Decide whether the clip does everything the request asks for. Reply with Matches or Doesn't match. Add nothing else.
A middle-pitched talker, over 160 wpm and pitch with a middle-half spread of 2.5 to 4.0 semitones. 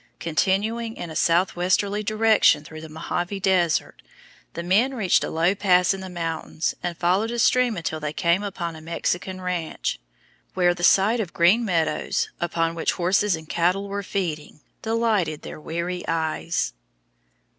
Doesn't match